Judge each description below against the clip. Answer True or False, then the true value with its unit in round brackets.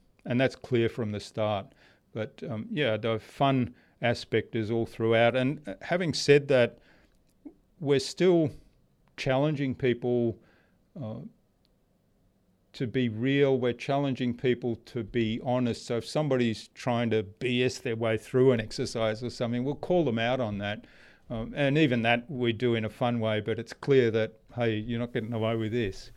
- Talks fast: False (165 wpm)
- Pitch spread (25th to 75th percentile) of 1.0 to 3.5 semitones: True (2.6 semitones)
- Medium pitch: False (120 Hz)